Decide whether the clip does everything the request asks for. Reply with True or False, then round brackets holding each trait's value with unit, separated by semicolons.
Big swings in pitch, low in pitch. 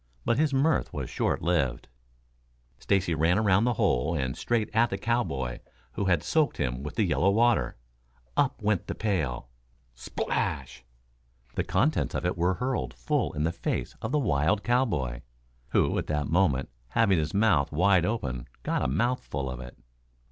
True (8.5 semitones; 90 Hz)